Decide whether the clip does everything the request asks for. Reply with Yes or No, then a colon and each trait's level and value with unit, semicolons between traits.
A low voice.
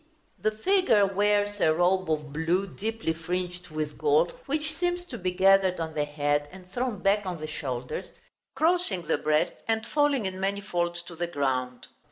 No: medium, 185 Hz